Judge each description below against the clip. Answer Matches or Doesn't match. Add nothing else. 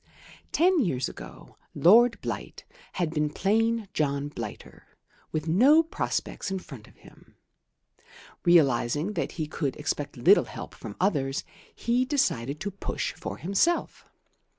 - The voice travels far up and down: Matches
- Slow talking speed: Matches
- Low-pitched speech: Doesn't match